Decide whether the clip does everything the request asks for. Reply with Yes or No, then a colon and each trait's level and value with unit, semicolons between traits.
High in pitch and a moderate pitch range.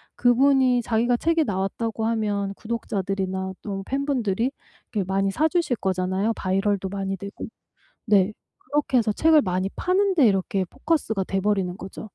Yes: high, 210 Hz; average, 4.5 semitones